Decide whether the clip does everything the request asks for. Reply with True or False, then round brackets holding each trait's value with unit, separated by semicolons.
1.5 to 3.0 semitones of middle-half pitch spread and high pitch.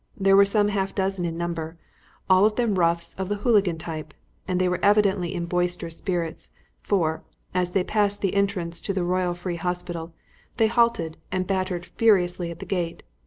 False (2.6 semitones; 180 Hz)